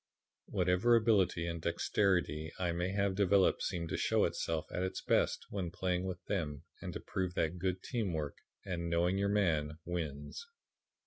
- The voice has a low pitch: Yes, very low, 90 Hz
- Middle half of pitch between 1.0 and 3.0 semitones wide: Yes, narrow, 2.5 semitones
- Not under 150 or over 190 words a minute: Yes, average, 170 wpm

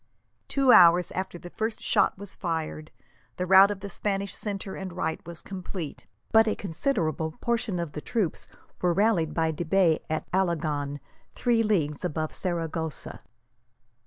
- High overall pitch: No, medium, 180 Hz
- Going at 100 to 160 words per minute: Yes, average, 155 wpm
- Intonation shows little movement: No, average, 3.7 semitones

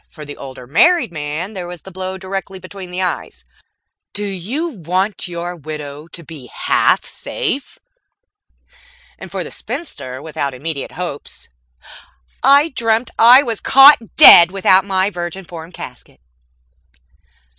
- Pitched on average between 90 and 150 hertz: No, medium, 185 Hz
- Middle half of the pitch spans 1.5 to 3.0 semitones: No, average, 4.5 semitones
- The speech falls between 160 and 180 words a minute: No, slow, 135 wpm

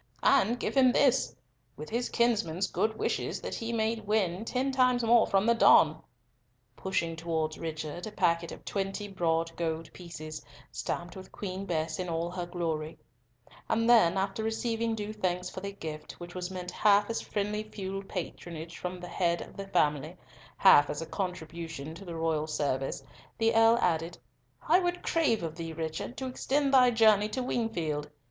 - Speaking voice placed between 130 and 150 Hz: No, medium, 185 Hz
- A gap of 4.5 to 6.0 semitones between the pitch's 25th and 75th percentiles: Yes, average, 5.3 semitones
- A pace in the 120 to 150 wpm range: No, average, 175 wpm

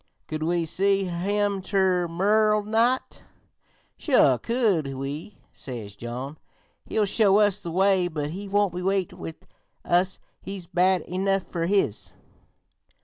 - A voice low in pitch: No, medium, 185 Hz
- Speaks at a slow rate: Yes, slow, 130 wpm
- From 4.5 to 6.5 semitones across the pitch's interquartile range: No, average, 3.4 semitones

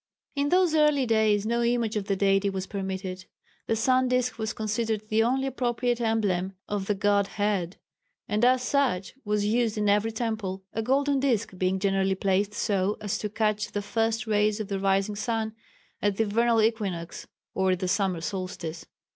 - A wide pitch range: No, average, 3.0 semitones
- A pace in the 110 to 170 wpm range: No, average, 180 wpm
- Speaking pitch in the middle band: No, high, 210 Hz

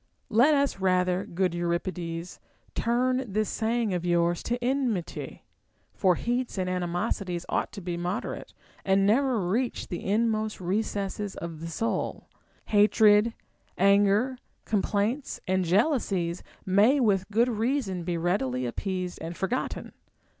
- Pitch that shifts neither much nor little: Yes, average, 4.4 semitones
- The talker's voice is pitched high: Yes, high, 195 Hz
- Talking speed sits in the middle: No, slow, 130 wpm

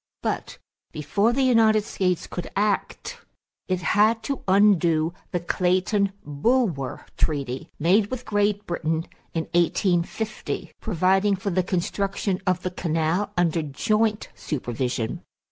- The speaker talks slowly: Yes, slow, 120 wpm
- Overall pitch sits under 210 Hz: Yes, medium, 185 Hz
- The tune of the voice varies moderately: Yes, average, 4.1 semitones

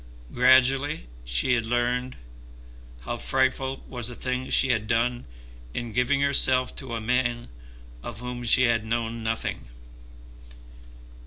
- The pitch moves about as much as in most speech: No, narrow, 2.0 semitones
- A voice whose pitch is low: Yes, low, 120 Hz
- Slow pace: Yes, slow, 130 wpm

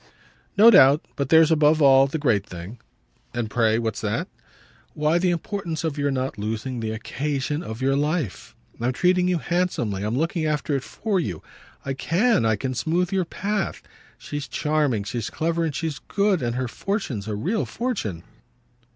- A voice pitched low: No, medium, 145 Hz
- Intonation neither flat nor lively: No, wide, 6.3 semitones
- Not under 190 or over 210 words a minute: No, average, 175 wpm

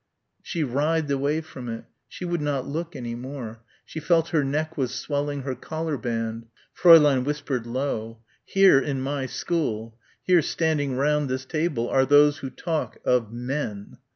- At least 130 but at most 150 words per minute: No, average, 165 wpm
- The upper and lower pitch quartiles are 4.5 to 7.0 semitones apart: No, average, 3.7 semitones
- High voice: No, medium, 140 Hz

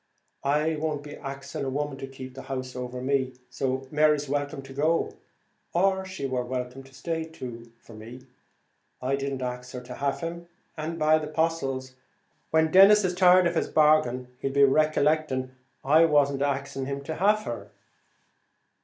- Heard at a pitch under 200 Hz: Yes, medium, 140 Hz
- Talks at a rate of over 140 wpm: Yes, average, 170 wpm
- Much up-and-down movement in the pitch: No, average, 3.3 semitones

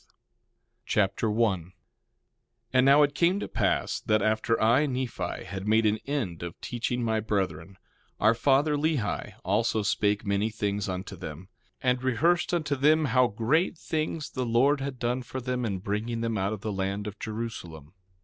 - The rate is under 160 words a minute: No, average, 180 wpm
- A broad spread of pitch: No, average, 4.4 semitones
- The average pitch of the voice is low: Yes, low, 115 Hz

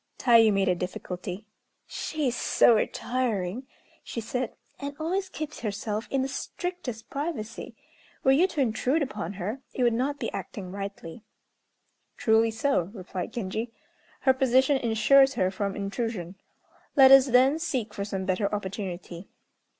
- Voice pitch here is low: No, high, 230 Hz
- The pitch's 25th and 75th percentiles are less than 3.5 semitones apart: No, average, 5.2 semitones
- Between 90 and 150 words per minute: Yes, average, 145 wpm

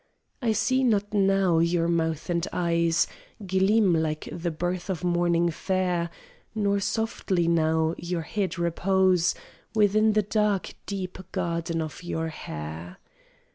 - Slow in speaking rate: Yes, slow, 130 wpm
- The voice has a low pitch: No, medium, 175 Hz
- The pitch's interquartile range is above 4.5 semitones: No, average, 2.8 semitones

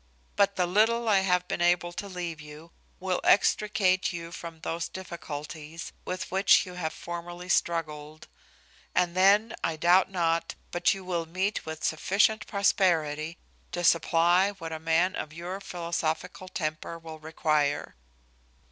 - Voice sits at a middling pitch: Yes, medium, 175 Hz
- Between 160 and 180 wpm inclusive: No, average, 145 wpm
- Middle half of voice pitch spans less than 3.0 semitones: Yes, narrow, 2.6 semitones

